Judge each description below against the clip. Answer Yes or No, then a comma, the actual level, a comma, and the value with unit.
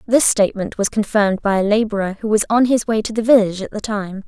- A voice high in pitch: Yes, high, 210 Hz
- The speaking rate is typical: No, fast, 255 wpm